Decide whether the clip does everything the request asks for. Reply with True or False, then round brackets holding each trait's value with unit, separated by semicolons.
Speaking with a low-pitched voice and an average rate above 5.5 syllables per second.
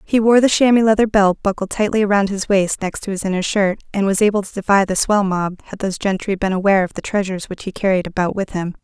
False (200 Hz; 6.3 syllables/s)